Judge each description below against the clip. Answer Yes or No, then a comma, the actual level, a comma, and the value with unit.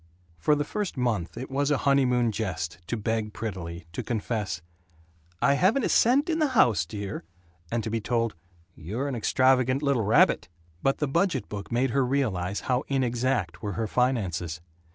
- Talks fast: No, average, 175 wpm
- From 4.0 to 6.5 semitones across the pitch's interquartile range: Yes, average, 4.9 semitones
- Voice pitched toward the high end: No, low, 120 Hz